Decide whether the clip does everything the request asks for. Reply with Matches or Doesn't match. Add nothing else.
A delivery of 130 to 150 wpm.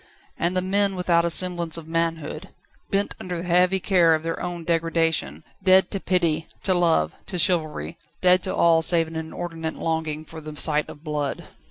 Doesn't match